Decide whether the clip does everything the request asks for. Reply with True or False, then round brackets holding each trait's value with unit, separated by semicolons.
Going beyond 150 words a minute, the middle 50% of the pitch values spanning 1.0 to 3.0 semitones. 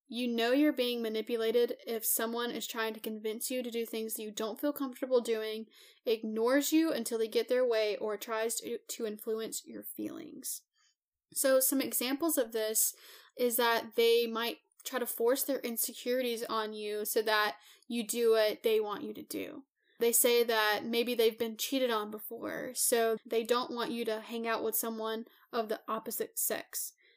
True (185 wpm; 2.7 semitones)